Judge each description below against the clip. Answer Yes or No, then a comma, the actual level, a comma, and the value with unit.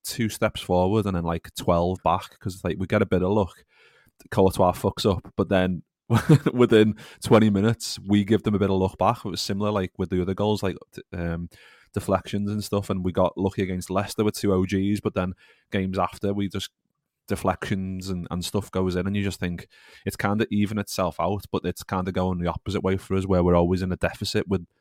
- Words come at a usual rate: No, fast, 225 wpm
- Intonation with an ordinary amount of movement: No, narrow, 2.1 semitones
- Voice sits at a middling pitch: No, very low, 95 Hz